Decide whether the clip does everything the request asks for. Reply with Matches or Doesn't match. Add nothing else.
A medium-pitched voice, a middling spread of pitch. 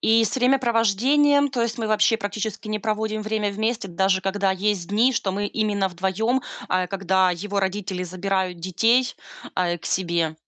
Doesn't match